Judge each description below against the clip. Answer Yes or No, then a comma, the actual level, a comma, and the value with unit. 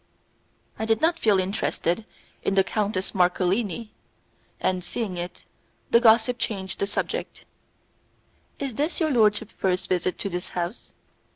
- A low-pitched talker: No, high, 200 Hz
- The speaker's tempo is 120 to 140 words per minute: Yes, slow, 135 wpm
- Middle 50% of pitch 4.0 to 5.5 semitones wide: No, average, 3.5 semitones